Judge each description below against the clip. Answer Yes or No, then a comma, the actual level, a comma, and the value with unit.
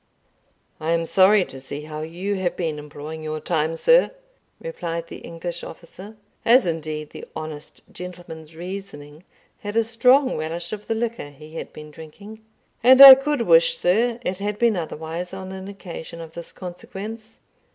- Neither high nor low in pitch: Yes, medium, 175 Hz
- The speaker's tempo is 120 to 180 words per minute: Yes, average, 165 wpm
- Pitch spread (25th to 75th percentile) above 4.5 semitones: Yes, average, 5.2 semitones